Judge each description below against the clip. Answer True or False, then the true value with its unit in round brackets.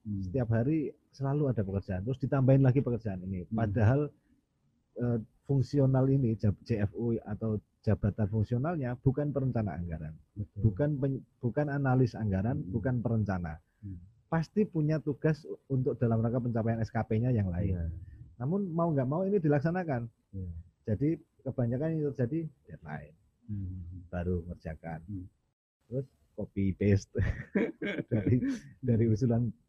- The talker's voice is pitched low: True (115 Hz)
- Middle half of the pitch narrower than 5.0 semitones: False (5.5 semitones)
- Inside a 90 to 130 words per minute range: True (115 wpm)